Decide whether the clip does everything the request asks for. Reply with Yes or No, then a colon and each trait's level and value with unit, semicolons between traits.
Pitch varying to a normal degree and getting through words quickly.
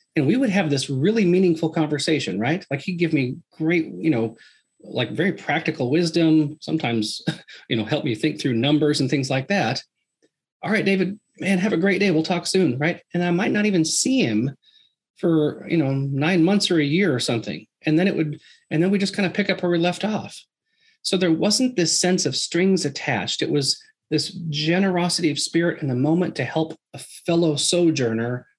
Yes: average, 3.7 semitones; fast, 210 wpm